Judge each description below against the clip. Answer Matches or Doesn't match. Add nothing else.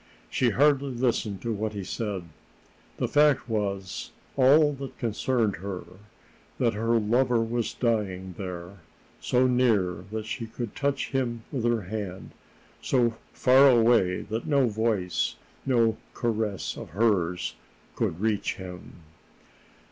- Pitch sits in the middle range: Doesn't match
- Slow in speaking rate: Matches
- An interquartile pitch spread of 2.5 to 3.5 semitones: Doesn't match